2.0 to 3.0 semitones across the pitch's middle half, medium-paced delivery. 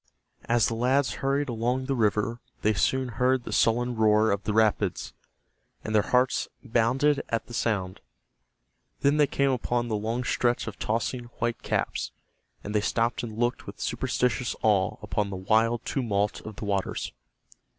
Yes: average, 2.7 semitones; average, 165 wpm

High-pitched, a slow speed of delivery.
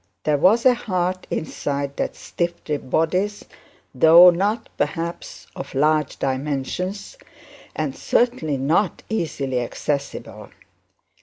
No: medium, 165 Hz; slow, 105 wpm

